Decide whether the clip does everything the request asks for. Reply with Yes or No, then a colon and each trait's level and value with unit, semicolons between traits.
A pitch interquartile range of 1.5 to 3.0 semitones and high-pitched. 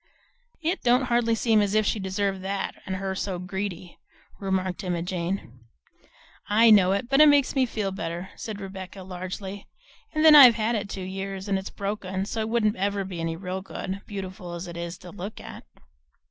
Yes: narrow, 2.5 semitones; high, 195 Hz